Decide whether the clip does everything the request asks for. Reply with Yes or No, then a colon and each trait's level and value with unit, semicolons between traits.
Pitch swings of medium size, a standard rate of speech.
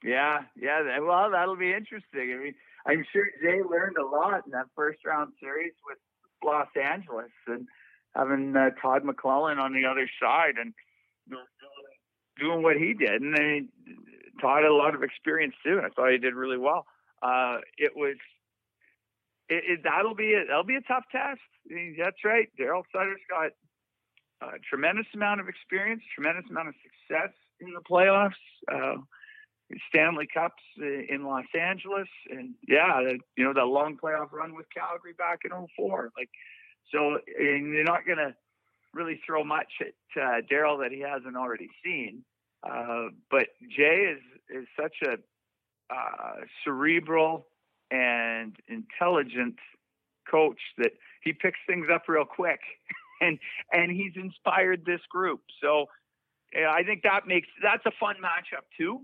No: wide, 5.7 semitones; average, 160 wpm